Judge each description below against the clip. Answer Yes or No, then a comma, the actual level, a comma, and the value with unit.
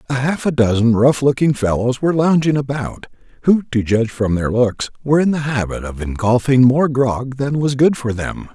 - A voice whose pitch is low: Yes, low, 130 Hz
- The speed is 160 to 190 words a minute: No, fast, 205 wpm